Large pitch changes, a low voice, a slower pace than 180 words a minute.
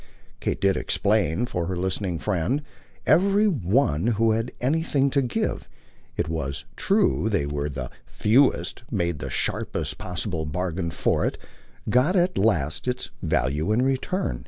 Yes: wide, 7.9 semitones; low, 100 Hz; average, 145 wpm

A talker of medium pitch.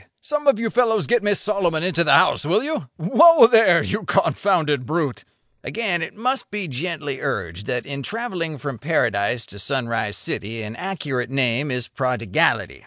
Yes: medium, 155 Hz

